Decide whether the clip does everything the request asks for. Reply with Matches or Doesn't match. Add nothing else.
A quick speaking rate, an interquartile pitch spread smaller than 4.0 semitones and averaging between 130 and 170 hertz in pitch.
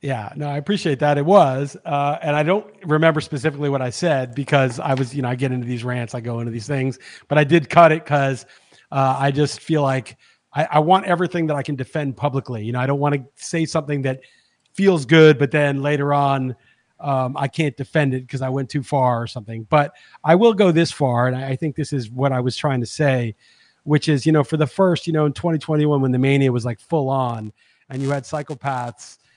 Matches